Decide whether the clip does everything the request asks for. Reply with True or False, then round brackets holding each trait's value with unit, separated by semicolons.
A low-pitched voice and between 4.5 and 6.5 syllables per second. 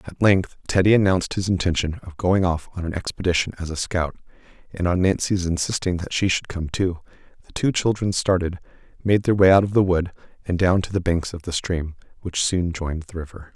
True (90 Hz; 5.7 syllables/s)